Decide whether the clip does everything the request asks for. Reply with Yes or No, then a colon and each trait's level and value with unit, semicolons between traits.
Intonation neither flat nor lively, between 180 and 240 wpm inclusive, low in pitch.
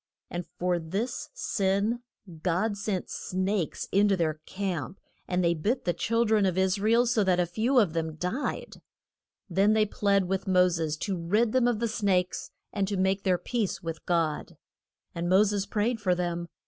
No: average, 3.3 semitones; average, 185 wpm; high, 190 Hz